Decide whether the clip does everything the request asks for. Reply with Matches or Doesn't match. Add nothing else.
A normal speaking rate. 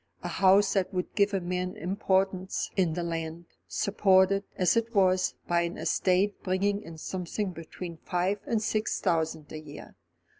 Matches